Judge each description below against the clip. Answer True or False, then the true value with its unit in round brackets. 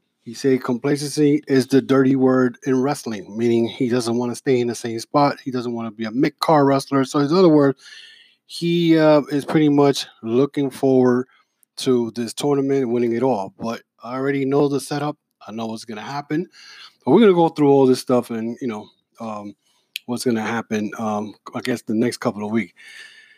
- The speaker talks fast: True (210 wpm)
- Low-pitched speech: True (130 Hz)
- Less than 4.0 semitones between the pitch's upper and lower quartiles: True (3.6 semitones)